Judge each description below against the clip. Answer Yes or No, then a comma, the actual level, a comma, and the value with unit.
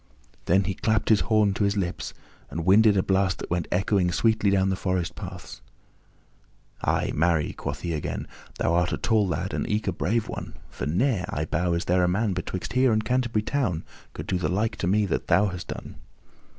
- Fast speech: Yes, fast, 210 wpm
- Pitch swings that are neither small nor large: Yes, average, 3.4 semitones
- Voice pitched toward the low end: Yes, very low, 95 Hz